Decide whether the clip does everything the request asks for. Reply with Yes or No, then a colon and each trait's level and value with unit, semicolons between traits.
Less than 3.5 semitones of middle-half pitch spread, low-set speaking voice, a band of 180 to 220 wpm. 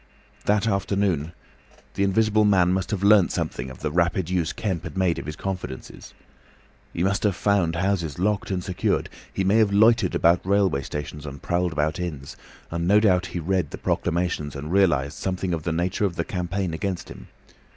Yes: average, 3.1 semitones; very low, 90 Hz; average, 190 wpm